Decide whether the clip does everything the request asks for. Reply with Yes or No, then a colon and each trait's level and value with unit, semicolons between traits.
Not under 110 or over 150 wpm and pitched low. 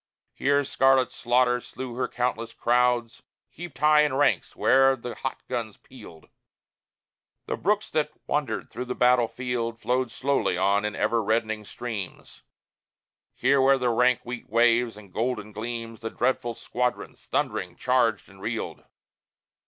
Yes: average, 140 wpm; low, 120 Hz